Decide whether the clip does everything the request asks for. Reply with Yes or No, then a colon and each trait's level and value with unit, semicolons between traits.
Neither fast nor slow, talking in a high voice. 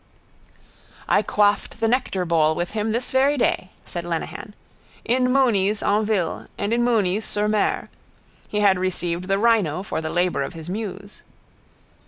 Yes: average, 155 wpm; high, 205 Hz